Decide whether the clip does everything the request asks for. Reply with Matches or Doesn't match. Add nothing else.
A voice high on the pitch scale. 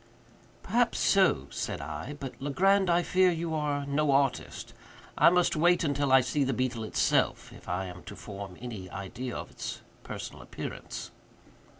Doesn't match